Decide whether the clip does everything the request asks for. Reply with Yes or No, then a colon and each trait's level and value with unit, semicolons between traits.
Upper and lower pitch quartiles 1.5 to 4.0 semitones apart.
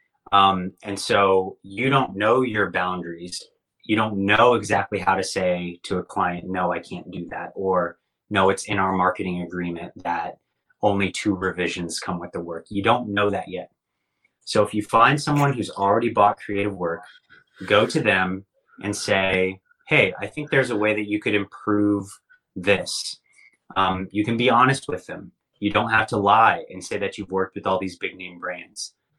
Yes: narrow, 2.5 semitones